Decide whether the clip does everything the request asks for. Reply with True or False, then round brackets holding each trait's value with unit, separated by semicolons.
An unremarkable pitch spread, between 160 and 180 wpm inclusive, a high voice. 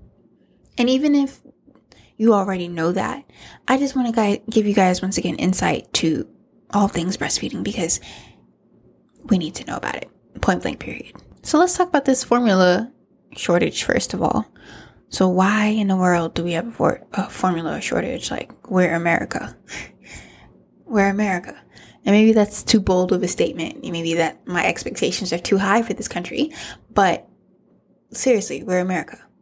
True (4.4 semitones; 165 wpm; 200 Hz)